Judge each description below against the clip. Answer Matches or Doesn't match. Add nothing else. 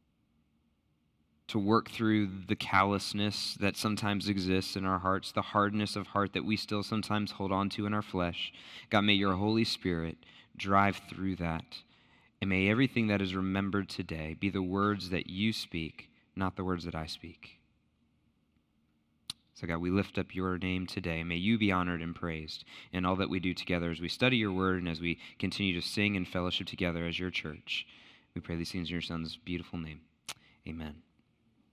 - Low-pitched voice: Matches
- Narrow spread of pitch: Doesn't match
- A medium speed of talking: Matches